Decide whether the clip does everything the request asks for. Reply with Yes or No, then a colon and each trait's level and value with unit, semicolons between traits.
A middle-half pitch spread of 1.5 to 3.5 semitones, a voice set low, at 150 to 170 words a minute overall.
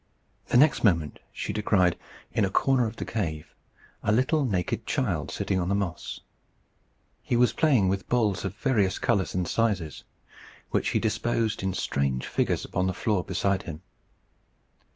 No: average, 3.9 semitones; low, 100 Hz; average, 160 wpm